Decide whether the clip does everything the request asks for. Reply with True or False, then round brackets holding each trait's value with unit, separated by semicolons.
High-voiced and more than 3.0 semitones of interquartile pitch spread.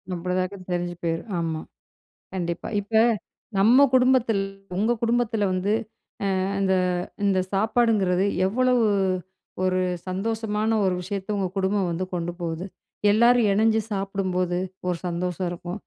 True (195 Hz; 3.5 semitones)